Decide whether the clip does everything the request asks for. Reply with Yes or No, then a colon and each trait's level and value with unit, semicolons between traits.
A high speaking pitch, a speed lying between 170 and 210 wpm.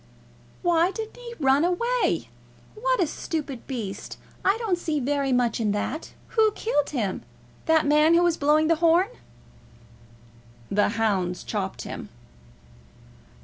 No: very high, 310 Hz; average, 140 wpm